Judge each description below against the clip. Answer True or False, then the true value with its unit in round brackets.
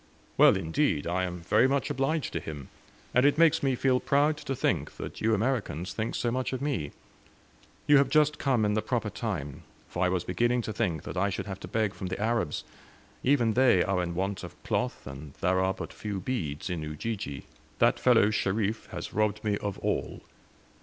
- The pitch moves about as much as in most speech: False (6.0 semitones)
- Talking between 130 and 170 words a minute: False (205 wpm)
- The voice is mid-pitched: False (105 Hz)